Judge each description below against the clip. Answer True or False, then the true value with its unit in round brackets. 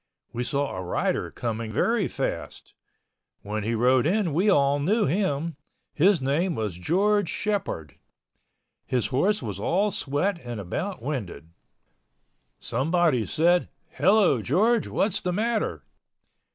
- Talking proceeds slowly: True (130 wpm)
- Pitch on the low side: False (150 Hz)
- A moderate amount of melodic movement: False (8.4 semitones)